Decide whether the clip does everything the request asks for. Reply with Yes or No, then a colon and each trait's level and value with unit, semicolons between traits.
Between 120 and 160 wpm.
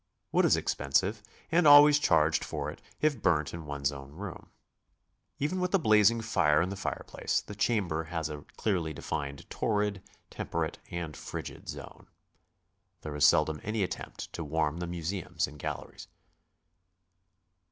Yes: average, 150 wpm